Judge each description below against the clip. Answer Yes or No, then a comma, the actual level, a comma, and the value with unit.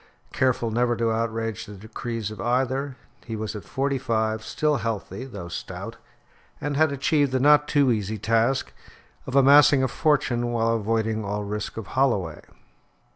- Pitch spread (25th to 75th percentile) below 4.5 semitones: Yes, average, 3.4 semitones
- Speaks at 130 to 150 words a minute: No, average, 160 wpm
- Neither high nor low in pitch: No, low, 115 Hz